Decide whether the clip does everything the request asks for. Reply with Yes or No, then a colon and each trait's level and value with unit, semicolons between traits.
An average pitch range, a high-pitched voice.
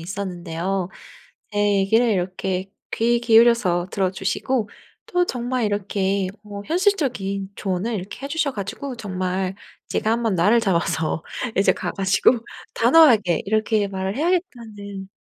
Yes: average, 3.8 semitones; high, 200 Hz